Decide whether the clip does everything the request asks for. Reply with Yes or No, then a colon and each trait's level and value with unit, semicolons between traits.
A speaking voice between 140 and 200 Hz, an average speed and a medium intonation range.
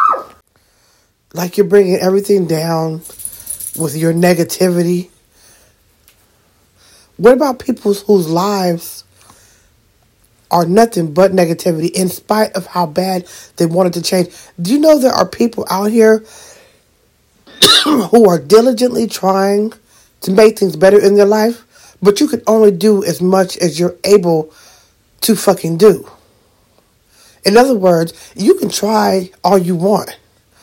No: medium, 185 Hz; slow, 130 wpm; average, 4.1 semitones